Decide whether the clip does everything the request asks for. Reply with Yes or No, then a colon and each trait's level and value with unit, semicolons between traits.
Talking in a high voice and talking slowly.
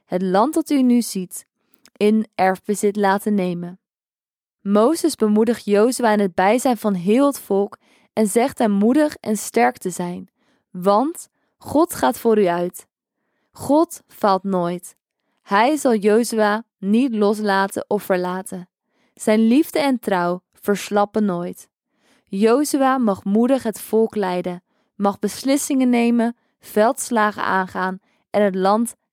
Yes: high, 215 Hz; slow, 130 wpm